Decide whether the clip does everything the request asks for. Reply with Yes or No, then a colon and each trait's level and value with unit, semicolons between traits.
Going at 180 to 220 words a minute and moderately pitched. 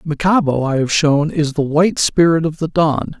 Yes: fast, 205 wpm; medium, 155 Hz